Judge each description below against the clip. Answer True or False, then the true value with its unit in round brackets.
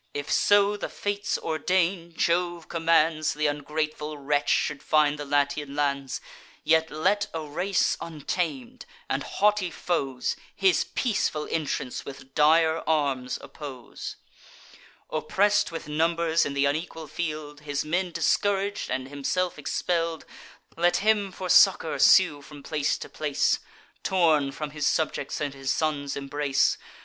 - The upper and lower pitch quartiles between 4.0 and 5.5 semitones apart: False (3.2 semitones)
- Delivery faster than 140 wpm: False (135 wpm)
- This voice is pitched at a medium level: True (155 Hz)